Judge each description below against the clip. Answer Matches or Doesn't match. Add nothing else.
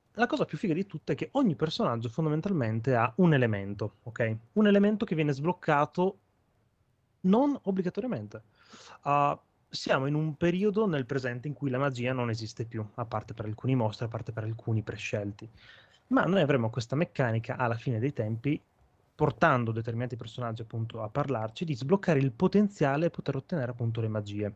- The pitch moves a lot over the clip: Matches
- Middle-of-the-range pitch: Doesn't match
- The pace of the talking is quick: Matches